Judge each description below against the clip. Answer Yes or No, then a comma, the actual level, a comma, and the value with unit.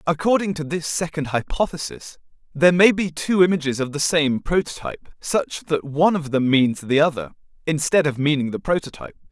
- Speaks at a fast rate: No, average, 175 wpm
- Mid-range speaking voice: Yes, medium, 155 Hz